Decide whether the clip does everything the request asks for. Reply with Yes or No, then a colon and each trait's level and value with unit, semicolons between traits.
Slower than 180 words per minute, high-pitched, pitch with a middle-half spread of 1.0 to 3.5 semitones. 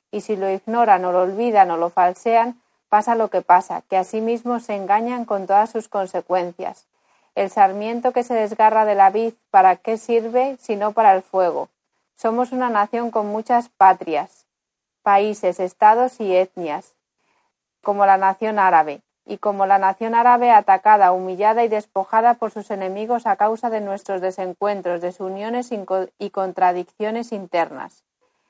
Yes: average, 160 wpm; high, 210 Hz; average, 3.2 semitones